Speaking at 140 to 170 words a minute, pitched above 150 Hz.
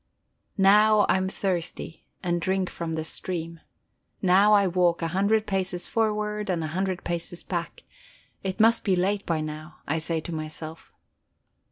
Yes: average, 160 wpm; medium, 185 Hz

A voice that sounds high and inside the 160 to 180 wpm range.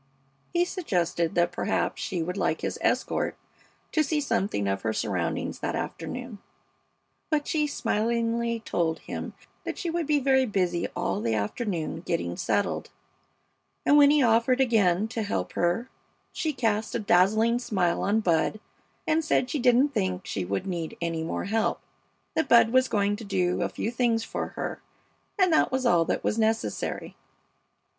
Yes: high, 220 Hz; average, 165 wpm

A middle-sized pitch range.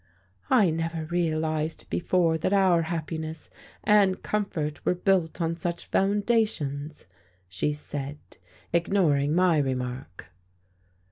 Yes: average, 3.5 semitones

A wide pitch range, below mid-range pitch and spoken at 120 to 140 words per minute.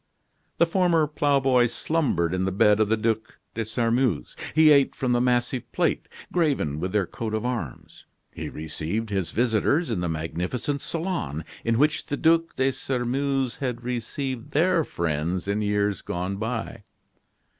No: wide, 5.8 semitones; low, 120 Hz; average, 155 wpm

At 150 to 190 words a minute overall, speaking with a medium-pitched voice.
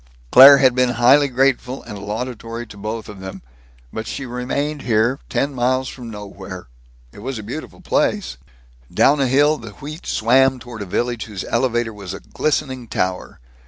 No: average, 170 wpm; low, 120 Hz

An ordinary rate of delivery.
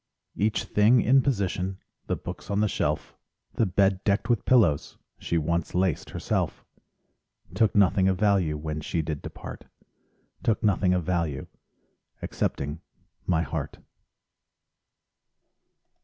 No: slow, 125 wpm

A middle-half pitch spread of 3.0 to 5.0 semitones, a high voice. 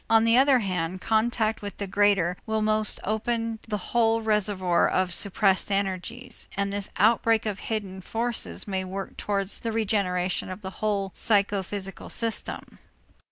No: narrow, 2.6 semitones; high, 205 Hz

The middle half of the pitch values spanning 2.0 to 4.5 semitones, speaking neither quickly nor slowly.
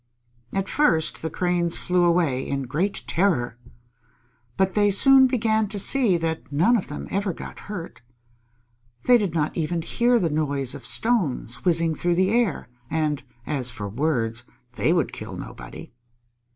No: wide, 5.4 semitones; average, 155 wpm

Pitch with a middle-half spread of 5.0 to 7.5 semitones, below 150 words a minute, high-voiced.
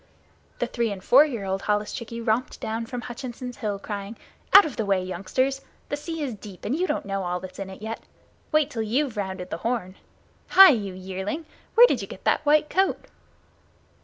No: wide, 5.5 semitones; average, 200 wpm; high, 225 Hz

